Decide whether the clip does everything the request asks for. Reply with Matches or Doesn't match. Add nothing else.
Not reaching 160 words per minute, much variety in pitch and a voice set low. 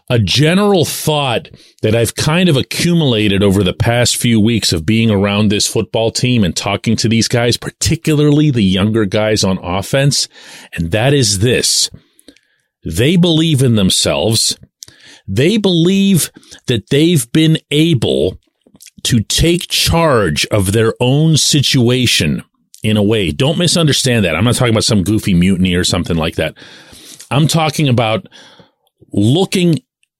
Matches